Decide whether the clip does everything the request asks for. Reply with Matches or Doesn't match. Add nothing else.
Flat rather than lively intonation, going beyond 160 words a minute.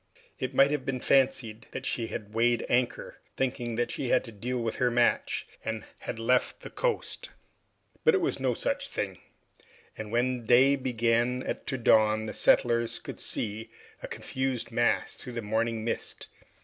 Matches